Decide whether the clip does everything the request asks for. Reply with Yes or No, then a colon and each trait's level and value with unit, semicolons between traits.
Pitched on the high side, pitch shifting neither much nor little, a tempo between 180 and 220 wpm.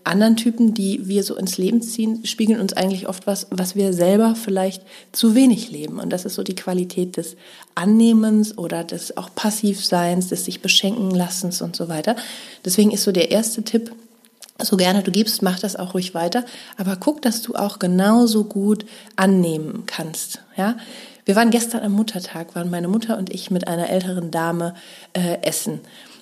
Yes: high, 200 Hz; average, 3.4 semitones; average, 185 wpm